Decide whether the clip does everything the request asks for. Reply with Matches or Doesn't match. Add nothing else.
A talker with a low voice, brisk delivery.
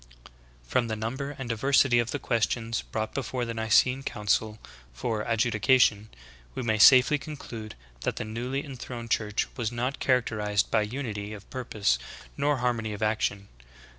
Doesn't match